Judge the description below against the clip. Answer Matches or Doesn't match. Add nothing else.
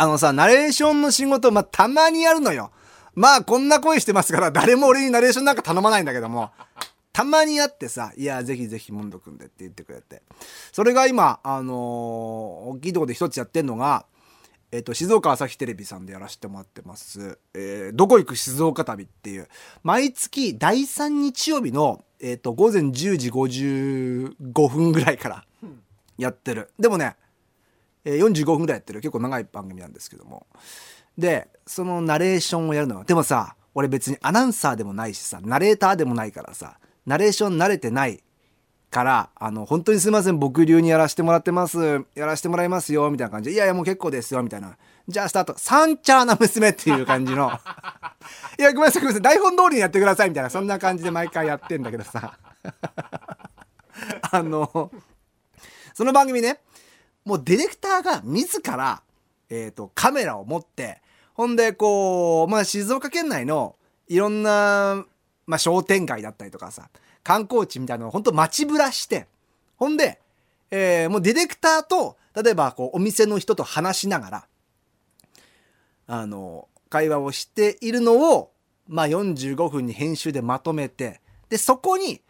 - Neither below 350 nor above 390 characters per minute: Matches